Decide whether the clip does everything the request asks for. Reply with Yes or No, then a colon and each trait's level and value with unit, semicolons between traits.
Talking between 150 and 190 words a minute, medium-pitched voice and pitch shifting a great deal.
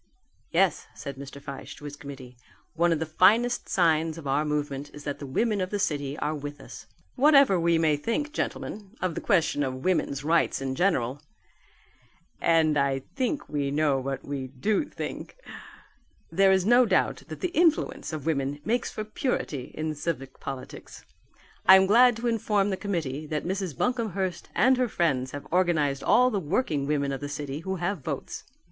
Yes: average, 180 wpm; medium, 160 Hz; wide, 6.0 semitones